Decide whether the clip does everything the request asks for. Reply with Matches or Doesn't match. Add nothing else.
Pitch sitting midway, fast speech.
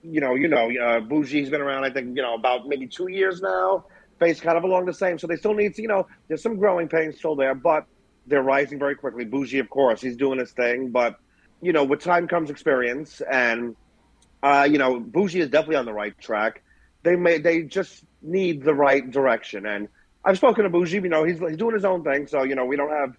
Matches